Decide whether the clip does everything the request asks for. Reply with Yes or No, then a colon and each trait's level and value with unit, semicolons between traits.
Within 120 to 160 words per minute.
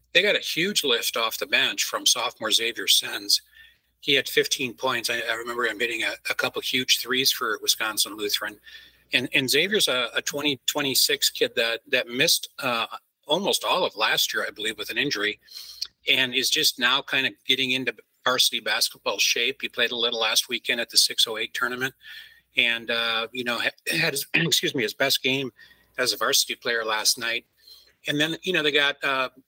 No: average, 195 wpm